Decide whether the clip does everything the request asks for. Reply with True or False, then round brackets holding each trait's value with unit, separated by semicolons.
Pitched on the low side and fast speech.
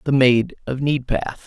False (130 Hz; 165 wpm)